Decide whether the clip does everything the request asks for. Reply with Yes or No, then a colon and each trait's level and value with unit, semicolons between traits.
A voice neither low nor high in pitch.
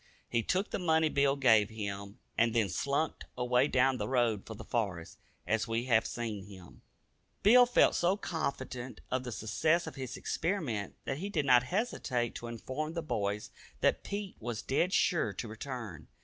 No: low, 125 Hz